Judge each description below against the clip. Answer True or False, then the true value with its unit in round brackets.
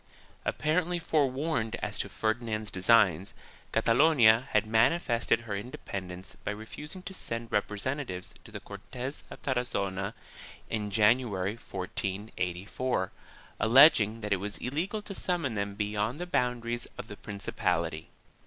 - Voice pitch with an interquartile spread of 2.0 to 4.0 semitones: False (4.5 semitones)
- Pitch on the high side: False (115 Hz)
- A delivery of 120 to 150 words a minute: True (135 wpm)